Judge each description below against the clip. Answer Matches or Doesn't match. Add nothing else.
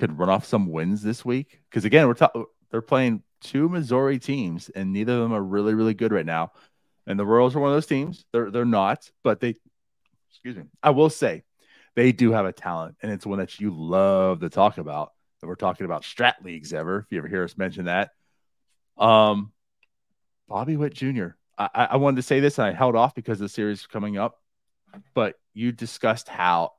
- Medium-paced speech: Doesn't match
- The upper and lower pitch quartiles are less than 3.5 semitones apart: Doesn't match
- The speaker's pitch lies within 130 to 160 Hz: Doesn't match